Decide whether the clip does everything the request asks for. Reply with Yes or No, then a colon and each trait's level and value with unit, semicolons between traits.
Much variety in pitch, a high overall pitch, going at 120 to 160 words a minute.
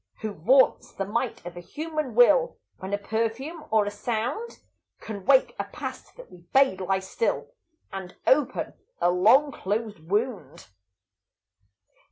Yes: wide, 5.8 semitones; high, 220 Hz; average, 145 wpm